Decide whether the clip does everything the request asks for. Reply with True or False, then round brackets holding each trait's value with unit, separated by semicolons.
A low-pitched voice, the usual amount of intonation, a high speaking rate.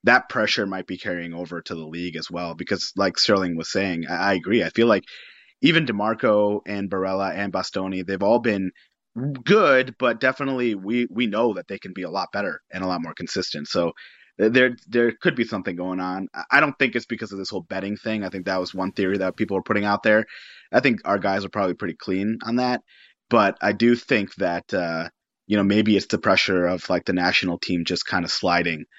True (100 Hz; 3.6 semitones; 225 wpm)